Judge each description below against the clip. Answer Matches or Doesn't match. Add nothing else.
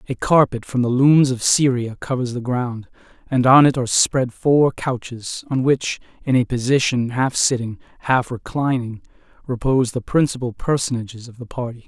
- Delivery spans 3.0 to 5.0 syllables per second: Matches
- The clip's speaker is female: Doesn't match